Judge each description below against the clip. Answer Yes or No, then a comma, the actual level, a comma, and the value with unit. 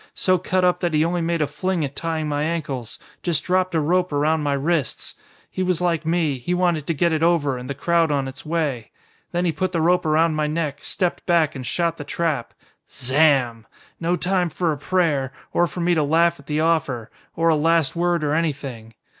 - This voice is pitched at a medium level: Yes, medium, 160 Hz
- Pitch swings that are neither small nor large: Yes, average, 3.1 semitones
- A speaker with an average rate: No, fast, 220 wpm